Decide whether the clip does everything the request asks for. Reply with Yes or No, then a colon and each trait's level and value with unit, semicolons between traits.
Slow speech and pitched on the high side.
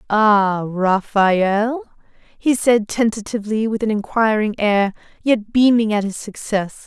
Yes: slow, 120 wpm; high, 215 Hz